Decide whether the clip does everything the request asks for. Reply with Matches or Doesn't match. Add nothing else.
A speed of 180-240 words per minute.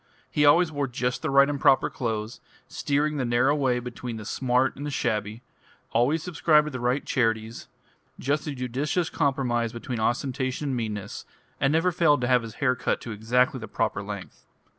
Matches